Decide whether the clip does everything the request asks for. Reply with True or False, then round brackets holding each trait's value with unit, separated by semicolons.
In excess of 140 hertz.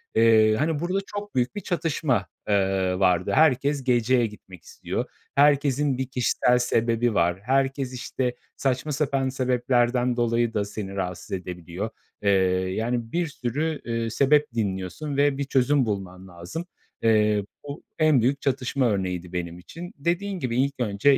False (125 Hz)